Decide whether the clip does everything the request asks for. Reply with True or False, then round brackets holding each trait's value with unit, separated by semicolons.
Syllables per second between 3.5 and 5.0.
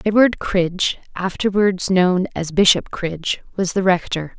True (4.5 syllables/s)